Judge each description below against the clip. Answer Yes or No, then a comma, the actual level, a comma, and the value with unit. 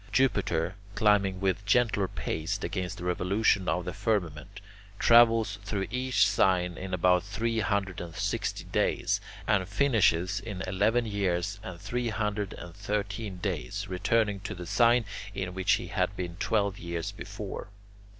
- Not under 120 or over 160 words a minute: Yes, average, 150 wpm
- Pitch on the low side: Yes, low, 100 Hz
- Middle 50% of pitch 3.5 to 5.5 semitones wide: No, average, 2.9 semitones